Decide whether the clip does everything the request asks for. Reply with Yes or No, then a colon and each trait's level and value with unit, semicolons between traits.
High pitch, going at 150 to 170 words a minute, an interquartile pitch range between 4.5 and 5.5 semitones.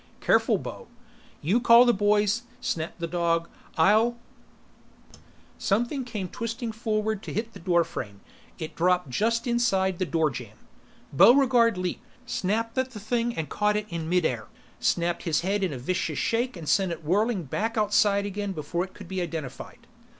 Yes: high, 195 Hz; average, 165 wpm; average, 5.2 semitones